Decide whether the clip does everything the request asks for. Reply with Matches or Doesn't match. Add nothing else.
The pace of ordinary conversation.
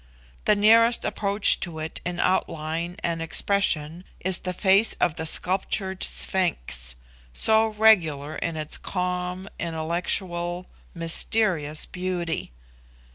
Doesn't match